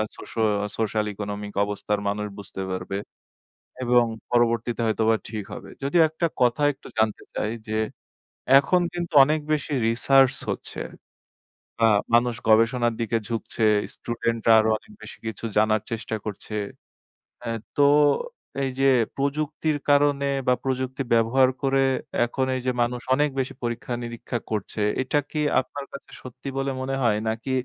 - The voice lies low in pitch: Yes, low, 120 Hz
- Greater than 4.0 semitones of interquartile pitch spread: No, average, 3.6 semitones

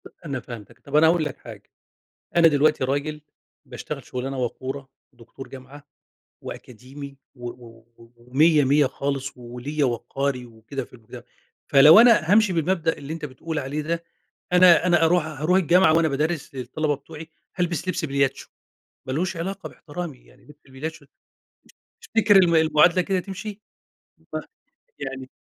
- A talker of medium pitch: Yes, medium, 150 Hz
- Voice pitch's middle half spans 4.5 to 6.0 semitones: No, average, 4.0 semitones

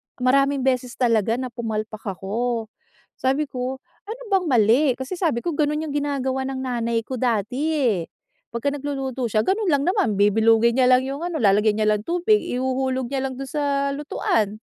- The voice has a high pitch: Yes, very high, 260 Hz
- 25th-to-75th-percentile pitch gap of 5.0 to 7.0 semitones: No, average, 3.7 semitones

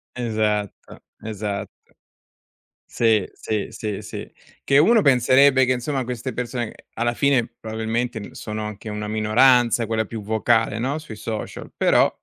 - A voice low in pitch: Yes, low, 115 Hz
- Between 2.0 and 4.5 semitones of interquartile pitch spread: Yes, average, 2.7 semitones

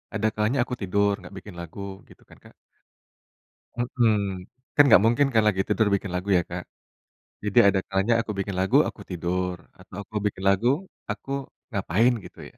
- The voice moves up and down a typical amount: Yes, average, 3.1 semitones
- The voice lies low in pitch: Yes, low, 100 Hz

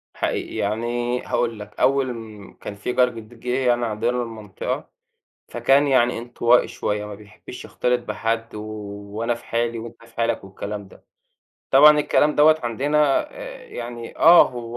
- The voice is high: No, low, 120 Hz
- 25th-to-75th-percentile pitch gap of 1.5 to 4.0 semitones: Yes, narrow, 2.4 semitones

